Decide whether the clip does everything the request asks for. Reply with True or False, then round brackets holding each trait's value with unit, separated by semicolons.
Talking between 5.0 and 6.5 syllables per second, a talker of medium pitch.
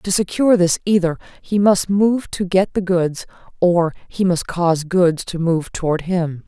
False (4.4 syllables/s; 180 Hz)